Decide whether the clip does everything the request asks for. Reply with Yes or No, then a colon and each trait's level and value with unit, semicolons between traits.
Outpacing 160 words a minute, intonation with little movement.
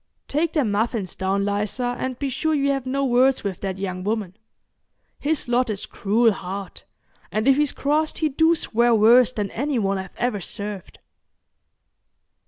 No: average, 170 wpm; average, 5.2 semitones